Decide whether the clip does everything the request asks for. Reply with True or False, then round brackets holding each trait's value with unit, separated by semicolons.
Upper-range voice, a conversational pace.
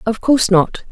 True (215 Hz; 195 wpm)